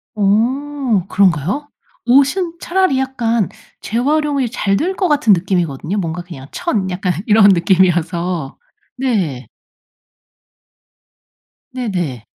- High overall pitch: Yes, high, 205 Hz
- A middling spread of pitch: No, wide, 7.2 semitones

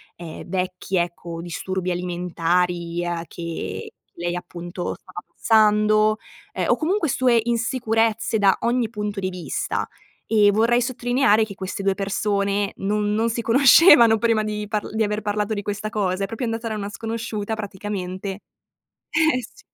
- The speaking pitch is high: Yes, high, 210 Hz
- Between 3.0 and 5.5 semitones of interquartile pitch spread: Yes, average, 3.4 semitones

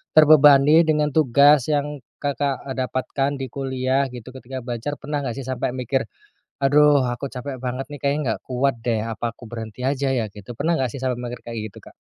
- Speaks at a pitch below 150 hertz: Yes, low, 135 Hz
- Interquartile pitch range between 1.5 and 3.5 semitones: Yes, narrow, 2.6 semitones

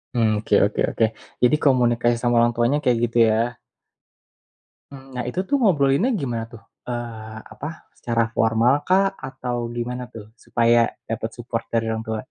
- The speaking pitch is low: Yes, low, 120 Hz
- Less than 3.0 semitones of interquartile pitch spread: Yes, narrow, 2.4 semitones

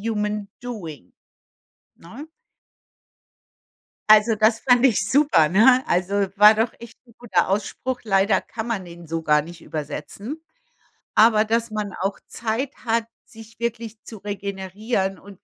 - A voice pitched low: No, high, 215 Hz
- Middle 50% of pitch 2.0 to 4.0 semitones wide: Yes, average, 3.1 semitones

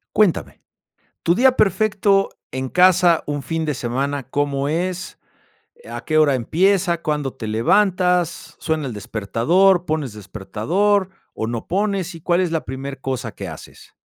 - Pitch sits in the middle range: Yes, medium, 160 Hz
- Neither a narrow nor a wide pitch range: No, wide, 5.7 semitones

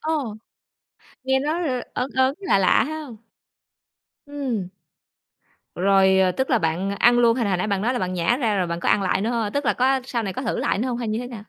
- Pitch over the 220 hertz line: Yes, high, 235 Hz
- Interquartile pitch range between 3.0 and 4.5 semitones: No, average, 5.1 semitones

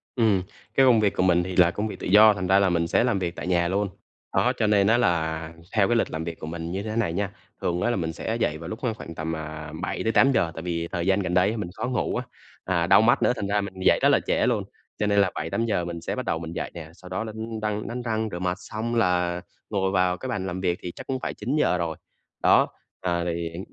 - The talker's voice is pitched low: Yes, very low, 95 Hz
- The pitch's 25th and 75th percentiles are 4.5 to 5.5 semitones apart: No, average, 4.0 semitones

